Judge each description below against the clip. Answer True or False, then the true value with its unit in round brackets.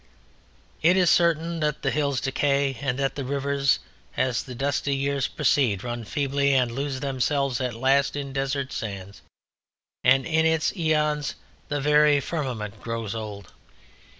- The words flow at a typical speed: True (145 wpm)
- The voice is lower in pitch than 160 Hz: True (140 Hz)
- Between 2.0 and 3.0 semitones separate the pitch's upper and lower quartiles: True (2.5 semitones)